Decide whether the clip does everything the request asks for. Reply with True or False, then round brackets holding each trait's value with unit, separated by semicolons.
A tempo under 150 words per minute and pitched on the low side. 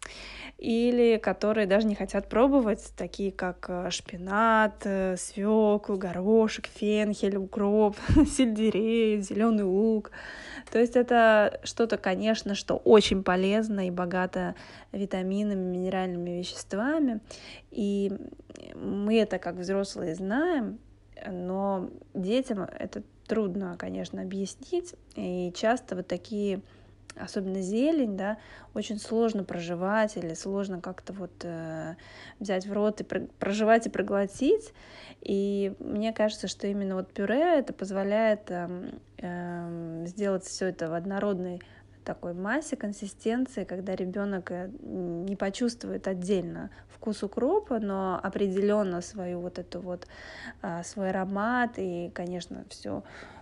False (110 wpm; 200 Hz)